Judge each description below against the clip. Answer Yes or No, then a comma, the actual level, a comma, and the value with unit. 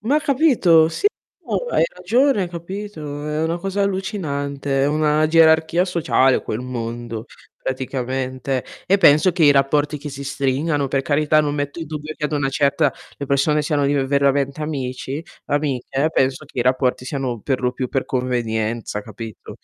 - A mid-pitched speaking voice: Yes, medium, 145 Hz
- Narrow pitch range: No, average, 3.3 semitones